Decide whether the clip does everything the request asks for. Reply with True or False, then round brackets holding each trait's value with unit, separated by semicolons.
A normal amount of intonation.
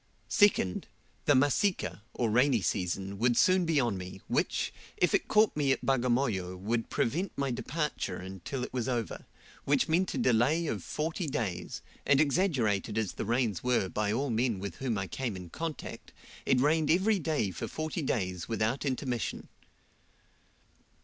False (6.3 semitones)